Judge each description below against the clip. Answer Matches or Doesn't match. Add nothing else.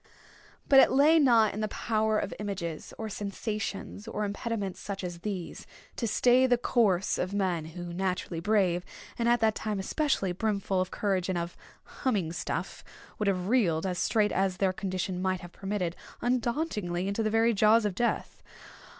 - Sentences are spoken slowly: Doesn't match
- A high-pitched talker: Matches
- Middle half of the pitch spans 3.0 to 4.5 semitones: Matches